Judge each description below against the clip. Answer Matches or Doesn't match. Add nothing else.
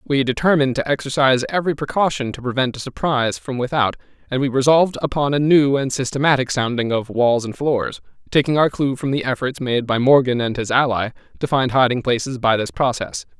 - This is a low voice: Matches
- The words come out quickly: Doesn't match